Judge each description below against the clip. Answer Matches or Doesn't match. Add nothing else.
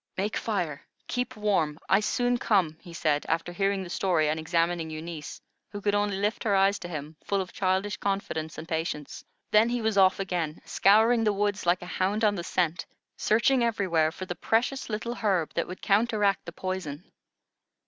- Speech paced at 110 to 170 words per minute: Doesn't match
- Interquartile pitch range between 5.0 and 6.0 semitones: Doesn't match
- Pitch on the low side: Doesn't match